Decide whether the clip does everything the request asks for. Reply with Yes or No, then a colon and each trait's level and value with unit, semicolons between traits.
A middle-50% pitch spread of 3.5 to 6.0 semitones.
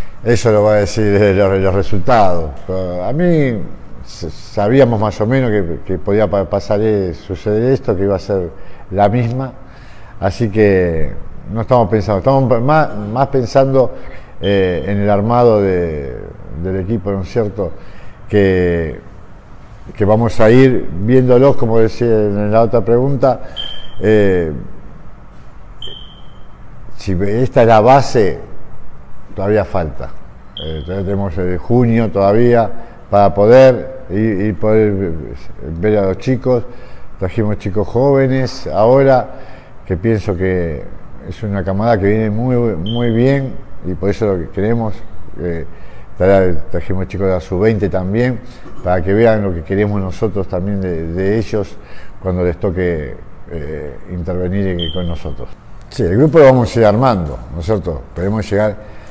Yes: average, 3.8 semitones